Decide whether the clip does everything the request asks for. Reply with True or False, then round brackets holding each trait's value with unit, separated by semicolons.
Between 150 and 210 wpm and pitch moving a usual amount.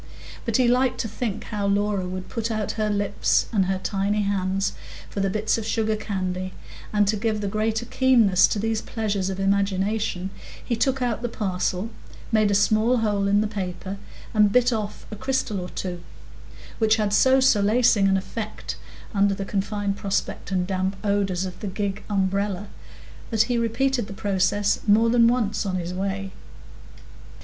False (175 wpm; 2.3 semitones)